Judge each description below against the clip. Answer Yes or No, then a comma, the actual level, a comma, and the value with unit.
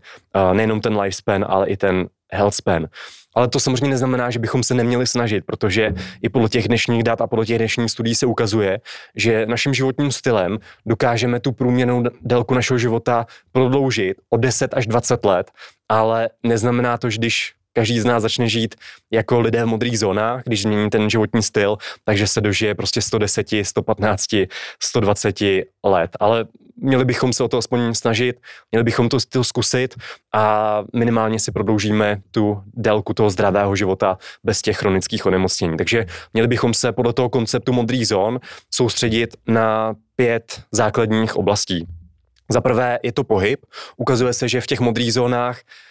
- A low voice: Yes, low, 115 Hz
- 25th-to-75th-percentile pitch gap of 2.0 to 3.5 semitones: Yes, narrow, 2.4 semitones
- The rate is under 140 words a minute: No, average, 165 wpm